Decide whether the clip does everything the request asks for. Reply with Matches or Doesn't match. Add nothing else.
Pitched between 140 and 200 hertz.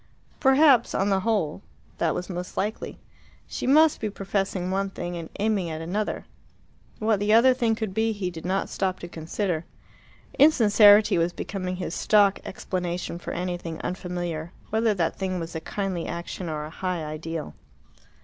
Matches